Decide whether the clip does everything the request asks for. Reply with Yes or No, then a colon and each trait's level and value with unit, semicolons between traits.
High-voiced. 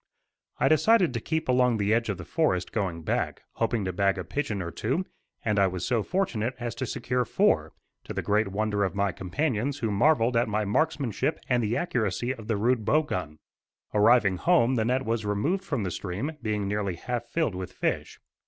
No: low, 115 Hz